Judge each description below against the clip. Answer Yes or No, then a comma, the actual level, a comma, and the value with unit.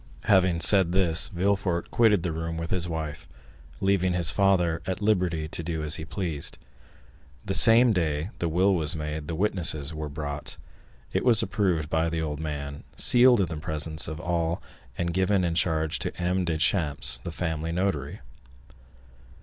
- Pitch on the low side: Yes, very low, 85 Hz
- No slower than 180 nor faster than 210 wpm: No, average, 165 wpm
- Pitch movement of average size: Yes, average, 3.2 semitones